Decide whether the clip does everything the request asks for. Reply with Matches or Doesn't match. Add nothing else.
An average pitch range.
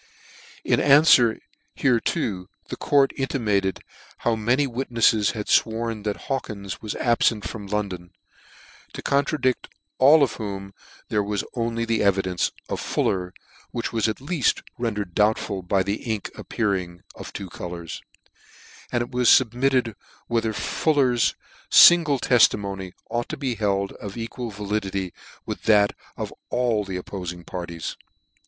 Matches